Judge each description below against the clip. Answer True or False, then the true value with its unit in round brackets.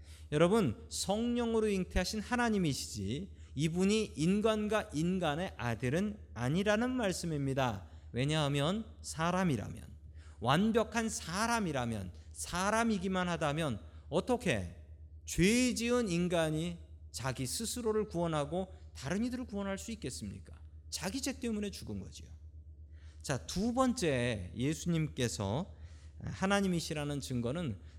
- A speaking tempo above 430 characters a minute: False (270 characters per minute)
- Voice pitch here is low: False (155 Hz)